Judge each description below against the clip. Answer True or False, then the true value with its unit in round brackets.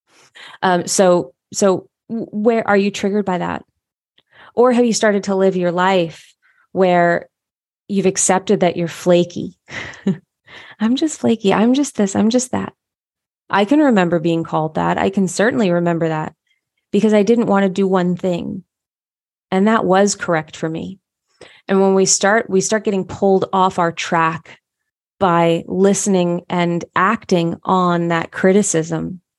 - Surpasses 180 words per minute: False (155 wpm)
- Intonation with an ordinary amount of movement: True (3.0 semitones)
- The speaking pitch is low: False (190 Hz)